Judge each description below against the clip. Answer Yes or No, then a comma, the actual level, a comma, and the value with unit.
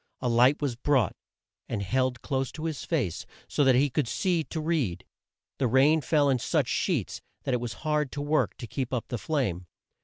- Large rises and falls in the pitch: No, average, 3.8 semitones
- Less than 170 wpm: No, average, 195 wpm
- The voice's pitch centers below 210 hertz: Yes, low, 135 Hz